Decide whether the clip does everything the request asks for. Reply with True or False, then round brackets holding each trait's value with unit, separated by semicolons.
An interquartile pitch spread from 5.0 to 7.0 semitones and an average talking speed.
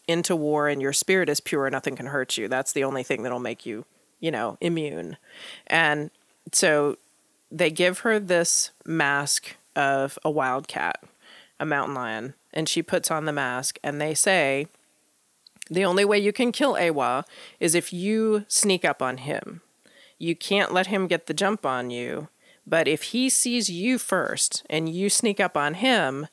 True (5.4 semitones; 180 wpm)